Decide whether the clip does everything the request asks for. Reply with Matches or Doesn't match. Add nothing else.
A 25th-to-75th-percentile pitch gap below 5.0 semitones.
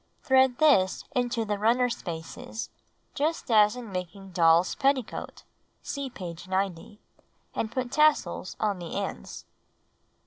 Doesn't match